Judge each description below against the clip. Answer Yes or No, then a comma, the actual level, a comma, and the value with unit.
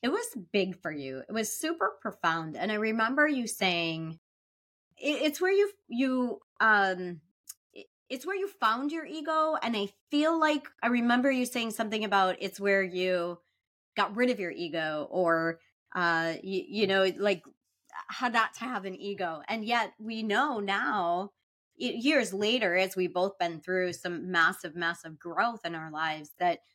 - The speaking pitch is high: Yes, high, 200 Hz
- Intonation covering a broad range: Yes, wide, 5.7 semitones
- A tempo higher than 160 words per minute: Yes, average, 170 wpm